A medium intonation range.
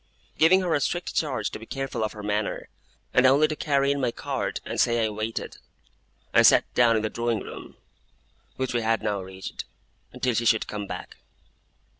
Yes: average, 4.2 semitones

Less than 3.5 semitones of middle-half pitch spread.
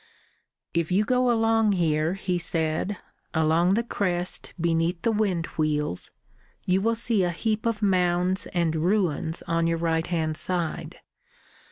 No: average, 3.9 semitones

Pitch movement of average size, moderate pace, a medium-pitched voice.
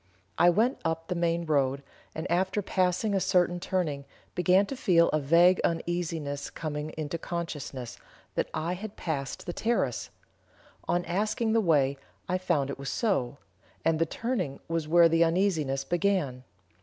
Yes: average, 3.7 semitones; average, 155 wpm; medium, 170 Hz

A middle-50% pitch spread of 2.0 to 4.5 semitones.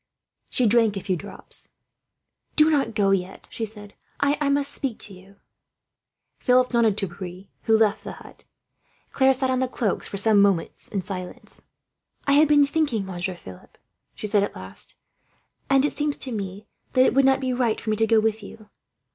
No: average, 5.0 semitones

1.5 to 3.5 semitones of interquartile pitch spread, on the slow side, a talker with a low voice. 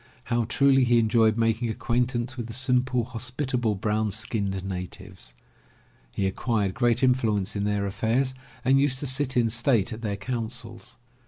No: average, 3.0 semitones; average, 155 wpm; low, 115 Hz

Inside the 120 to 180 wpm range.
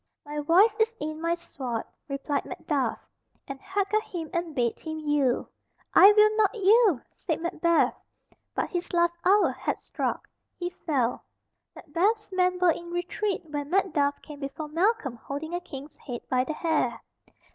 Yes: average, 160 wpm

